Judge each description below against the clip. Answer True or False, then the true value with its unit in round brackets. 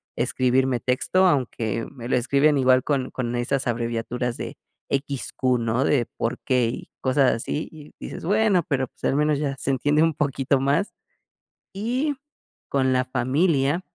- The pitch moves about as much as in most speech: True (3.0 semitones)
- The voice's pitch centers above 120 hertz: True (135 Hz)